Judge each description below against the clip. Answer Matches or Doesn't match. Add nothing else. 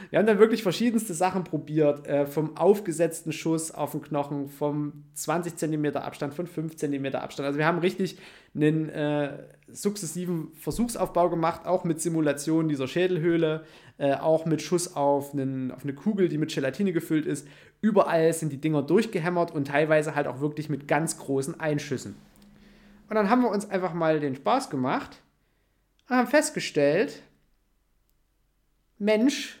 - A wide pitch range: Doesn't match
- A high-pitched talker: Doesn't match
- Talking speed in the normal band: Matches